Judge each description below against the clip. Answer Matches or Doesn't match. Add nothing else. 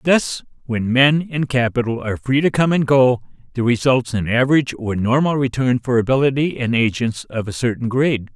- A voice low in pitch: Matches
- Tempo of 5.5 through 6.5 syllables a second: Matches